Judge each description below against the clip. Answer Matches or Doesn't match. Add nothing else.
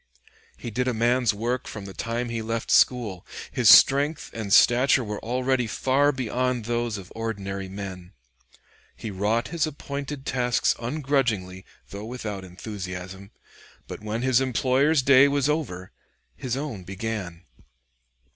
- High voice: Doesn't match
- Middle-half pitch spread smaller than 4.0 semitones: Doesn't match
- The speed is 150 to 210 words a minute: Doesn't match